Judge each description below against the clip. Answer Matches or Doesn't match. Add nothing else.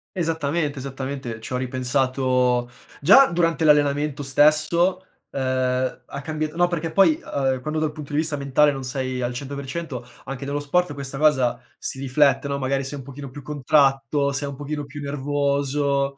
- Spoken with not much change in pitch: Matches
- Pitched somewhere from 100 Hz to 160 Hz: Matches